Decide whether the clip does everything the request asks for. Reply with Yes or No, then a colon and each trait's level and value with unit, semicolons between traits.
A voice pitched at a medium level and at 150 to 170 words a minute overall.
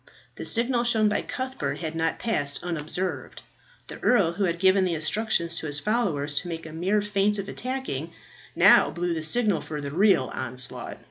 No: medium, 175 Hz; average, 180 wpm